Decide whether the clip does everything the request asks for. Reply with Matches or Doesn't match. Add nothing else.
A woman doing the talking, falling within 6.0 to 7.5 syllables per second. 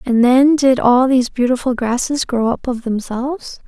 Doesn't match